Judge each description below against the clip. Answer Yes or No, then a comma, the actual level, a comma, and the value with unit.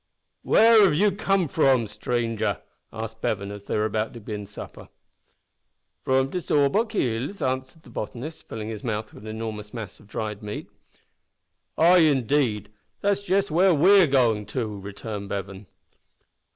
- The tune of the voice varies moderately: No, wide, 7.0 semitones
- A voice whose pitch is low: Yes, low, 115 Hz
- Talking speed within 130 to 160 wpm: Yes, average, 155 wpm